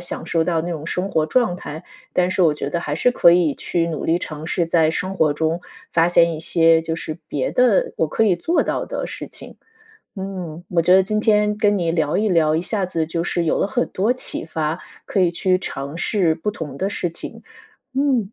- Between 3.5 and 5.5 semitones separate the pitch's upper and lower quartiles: No, average, 3.1 semitones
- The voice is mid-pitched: Yes, medium, 170 Hz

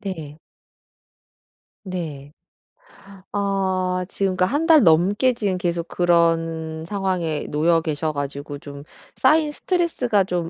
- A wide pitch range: No, average, 3.8 semitones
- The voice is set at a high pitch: No, medium, 175 Hz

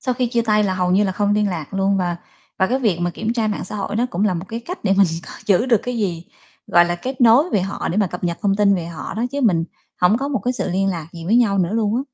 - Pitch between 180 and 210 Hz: Yes, high, 200 Hz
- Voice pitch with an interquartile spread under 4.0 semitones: No, average, 4.3 semitones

